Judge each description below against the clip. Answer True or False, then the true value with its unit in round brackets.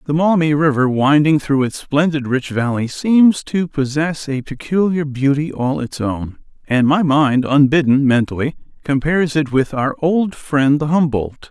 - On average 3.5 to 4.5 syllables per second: True (4.4 syllables/s)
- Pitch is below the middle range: False (145 Hz)